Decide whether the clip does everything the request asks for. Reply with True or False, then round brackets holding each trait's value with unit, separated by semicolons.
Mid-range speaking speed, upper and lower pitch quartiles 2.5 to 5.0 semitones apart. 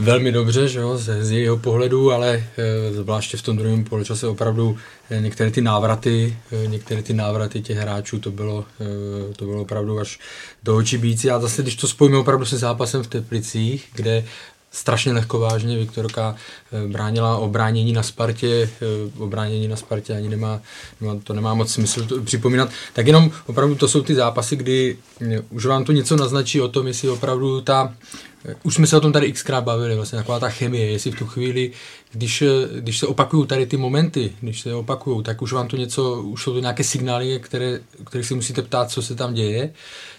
False (190 wpm; 2.8 semitones)